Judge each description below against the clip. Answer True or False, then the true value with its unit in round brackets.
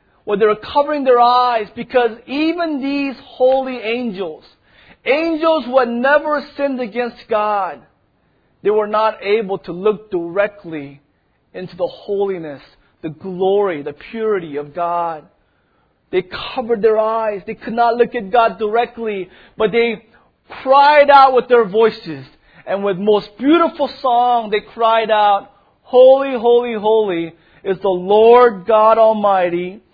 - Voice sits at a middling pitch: False (225 Hz)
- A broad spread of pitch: False (3.7 semitones)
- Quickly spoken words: False (135 wpm)